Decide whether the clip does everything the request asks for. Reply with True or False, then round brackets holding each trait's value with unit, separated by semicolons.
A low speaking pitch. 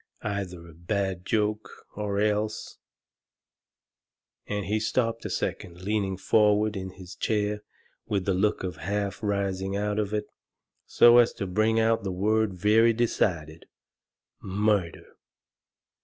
True (105 Hz)